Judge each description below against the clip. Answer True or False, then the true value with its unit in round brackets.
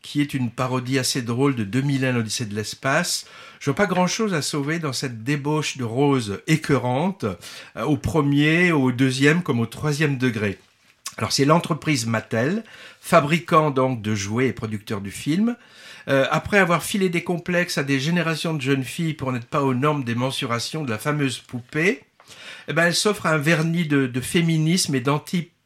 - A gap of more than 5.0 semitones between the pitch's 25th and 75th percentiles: False (4.4 semitones)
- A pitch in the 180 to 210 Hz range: False (145 Hz)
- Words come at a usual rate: True (180 wpm)